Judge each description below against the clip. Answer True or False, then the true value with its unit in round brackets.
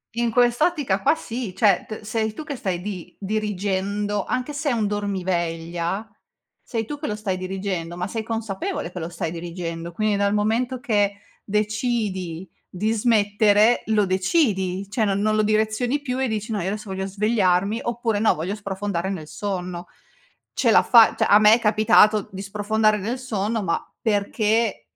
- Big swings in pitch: False (2.8 semitones)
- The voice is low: False (210 Hz)